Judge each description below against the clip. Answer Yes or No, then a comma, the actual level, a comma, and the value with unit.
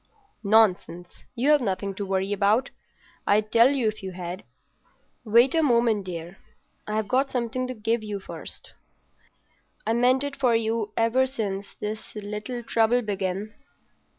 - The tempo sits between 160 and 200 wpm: No, average, 145 wpm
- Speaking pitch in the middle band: No, high, 220 Hz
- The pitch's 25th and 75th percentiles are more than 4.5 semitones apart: No, average, 3.3 semitones